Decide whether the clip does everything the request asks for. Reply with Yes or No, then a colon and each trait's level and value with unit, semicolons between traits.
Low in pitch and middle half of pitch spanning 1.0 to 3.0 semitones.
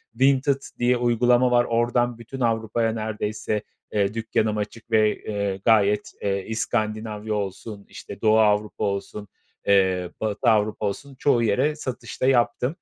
Yes: low, 110 Hz; narrow, 2.6 semitones